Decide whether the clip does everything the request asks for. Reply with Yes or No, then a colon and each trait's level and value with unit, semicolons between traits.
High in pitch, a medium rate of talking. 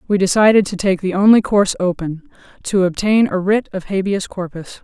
Yes: high, 195 Hz; average, 185 wpm